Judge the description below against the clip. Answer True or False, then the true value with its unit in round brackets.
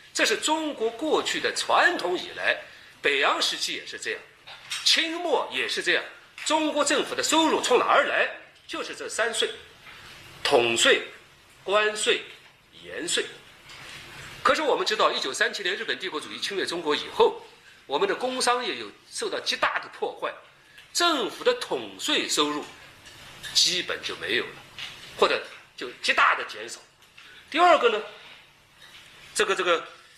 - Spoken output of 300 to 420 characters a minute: False (225 characters per minute)